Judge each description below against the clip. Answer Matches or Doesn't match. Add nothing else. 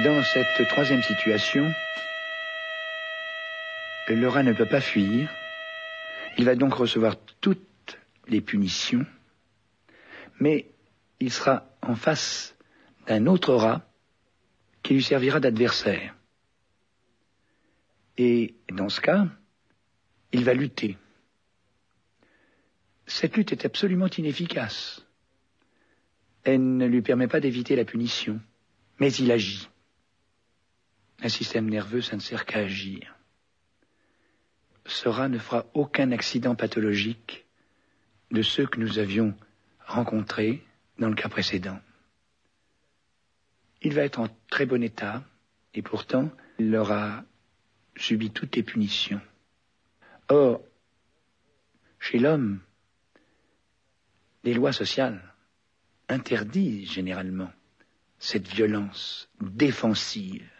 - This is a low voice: Matches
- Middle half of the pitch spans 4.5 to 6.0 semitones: Matches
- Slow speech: Matches